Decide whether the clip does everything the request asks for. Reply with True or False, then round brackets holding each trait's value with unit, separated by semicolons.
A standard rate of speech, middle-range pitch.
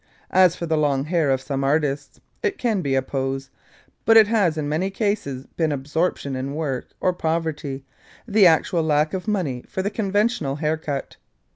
True (175 wpm; 155 Hz)